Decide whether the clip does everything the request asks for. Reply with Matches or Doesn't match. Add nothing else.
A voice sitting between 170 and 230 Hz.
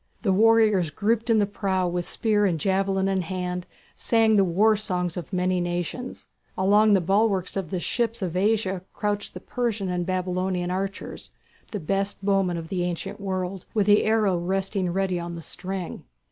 Matches